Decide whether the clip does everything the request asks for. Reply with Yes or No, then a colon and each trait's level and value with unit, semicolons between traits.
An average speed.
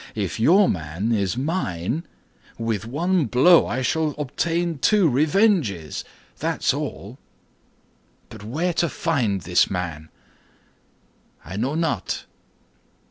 No: slow, 110 wpm